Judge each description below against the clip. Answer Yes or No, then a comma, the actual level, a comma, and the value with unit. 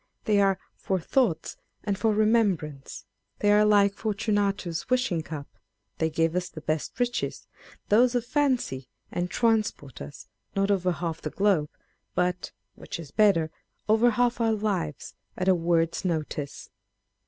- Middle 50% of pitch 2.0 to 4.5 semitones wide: No, average, 5.0 semitones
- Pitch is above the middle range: Yes, high, 195 Hz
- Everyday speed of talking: Yes, average, 160 wpm